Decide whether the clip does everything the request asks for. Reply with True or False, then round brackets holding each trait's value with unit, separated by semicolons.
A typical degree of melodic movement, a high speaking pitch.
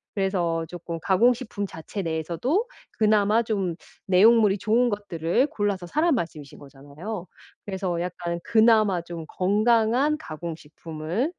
True (4.7 semitones; 195 Hz)